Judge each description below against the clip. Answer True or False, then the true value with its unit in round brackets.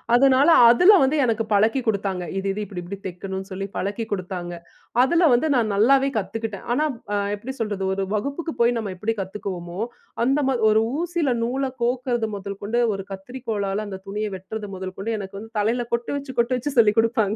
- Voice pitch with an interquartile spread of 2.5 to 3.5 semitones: False (4.2 semitones)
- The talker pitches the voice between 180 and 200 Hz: False (220 Hz)